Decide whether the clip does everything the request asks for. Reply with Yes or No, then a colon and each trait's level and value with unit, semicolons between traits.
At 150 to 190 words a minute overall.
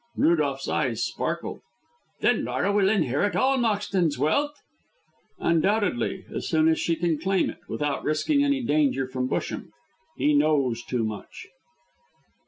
No: slow, 135 wpm